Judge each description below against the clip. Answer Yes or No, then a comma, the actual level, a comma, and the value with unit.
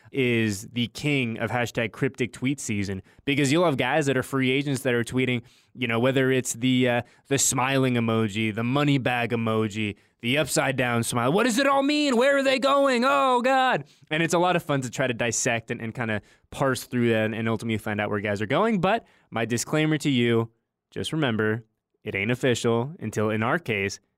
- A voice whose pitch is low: Yes, low, 125 Hz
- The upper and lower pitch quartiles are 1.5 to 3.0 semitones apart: No, average, 3.9 semitones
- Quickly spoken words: Yes, fast, 215 wpm